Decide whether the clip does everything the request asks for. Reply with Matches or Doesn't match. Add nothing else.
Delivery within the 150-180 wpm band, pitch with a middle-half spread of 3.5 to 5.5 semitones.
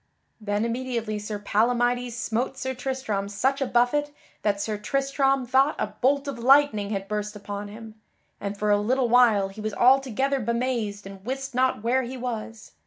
Matches